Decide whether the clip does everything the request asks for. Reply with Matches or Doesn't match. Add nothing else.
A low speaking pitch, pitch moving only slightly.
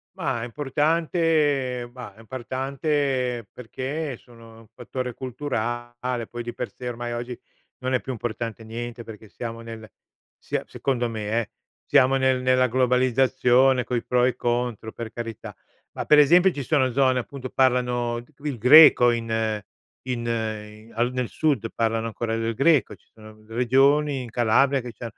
Matches